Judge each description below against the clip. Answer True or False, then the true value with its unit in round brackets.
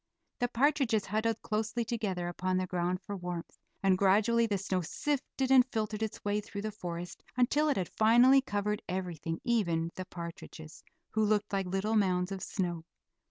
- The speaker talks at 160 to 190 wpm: True (170 wpm)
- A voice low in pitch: False (205 Hz)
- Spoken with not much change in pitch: False (3.8 semitones)